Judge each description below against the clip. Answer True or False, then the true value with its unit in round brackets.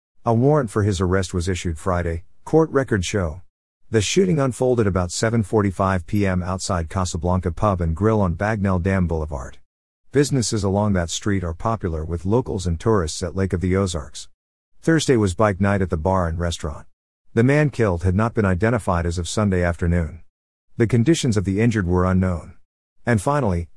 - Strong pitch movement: False (4.2 semitones)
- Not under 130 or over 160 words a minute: False (175 wpm)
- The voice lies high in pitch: False (95 Hz)